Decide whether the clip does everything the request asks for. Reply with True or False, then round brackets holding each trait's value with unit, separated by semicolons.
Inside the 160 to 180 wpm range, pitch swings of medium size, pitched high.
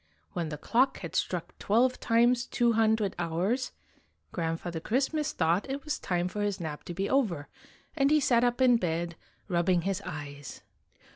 False (170 wpm; 6.2 semitones; 200 Hz)